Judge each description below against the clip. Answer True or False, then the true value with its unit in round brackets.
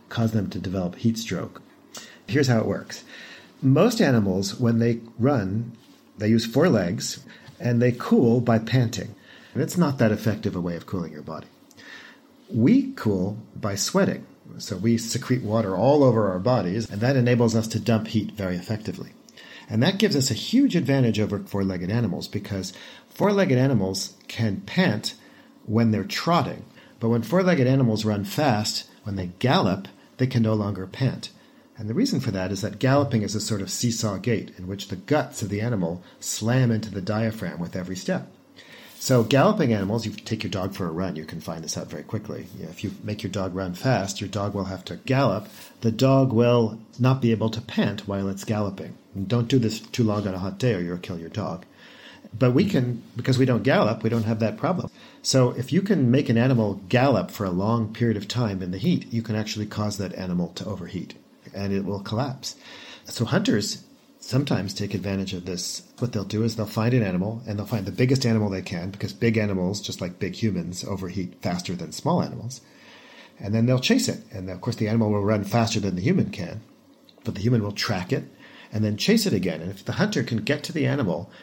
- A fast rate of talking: True (210 wpm)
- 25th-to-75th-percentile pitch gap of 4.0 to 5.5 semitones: False (3.6 semitones)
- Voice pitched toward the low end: True (110 Hz)